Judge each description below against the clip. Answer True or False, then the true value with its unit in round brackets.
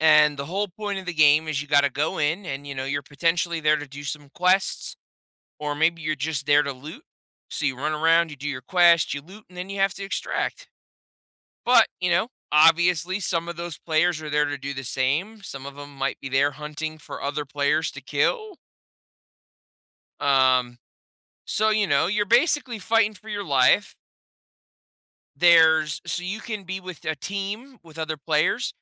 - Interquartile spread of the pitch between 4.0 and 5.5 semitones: True (4.5 semitones)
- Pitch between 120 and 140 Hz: False (160 Hz)